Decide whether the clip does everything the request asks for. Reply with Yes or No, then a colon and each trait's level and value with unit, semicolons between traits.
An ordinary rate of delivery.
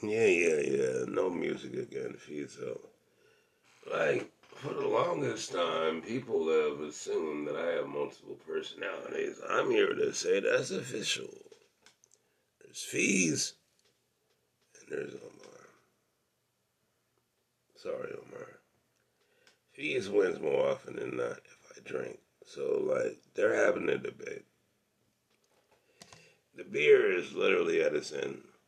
No: slow, 115 wpm